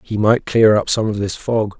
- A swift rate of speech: Yes, fast, 265 wpm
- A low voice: Yes, low, 105 Hz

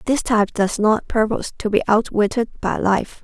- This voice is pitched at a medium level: No, high, 220 Hz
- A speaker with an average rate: Yes, average, 185 wpm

